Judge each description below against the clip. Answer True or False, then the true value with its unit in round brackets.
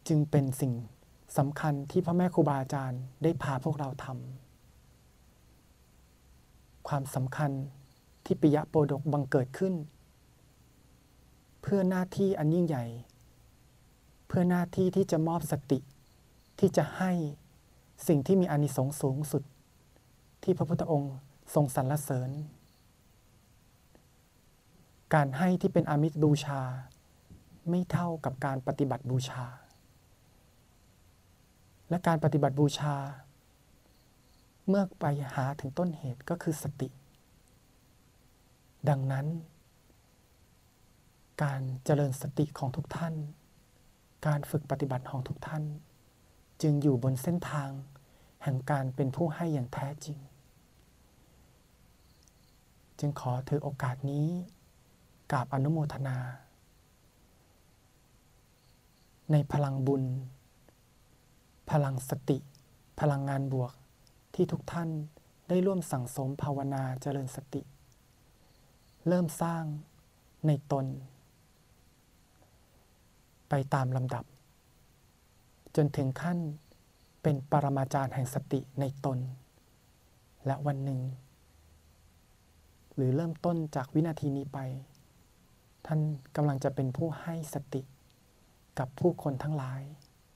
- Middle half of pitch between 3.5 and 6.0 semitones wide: False (2.9 semitones)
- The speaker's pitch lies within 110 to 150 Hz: True (140 Hz)